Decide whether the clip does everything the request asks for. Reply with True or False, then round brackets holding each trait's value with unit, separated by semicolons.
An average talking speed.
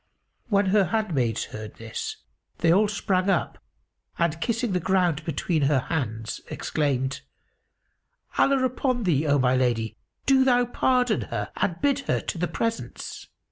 True (145 wpm)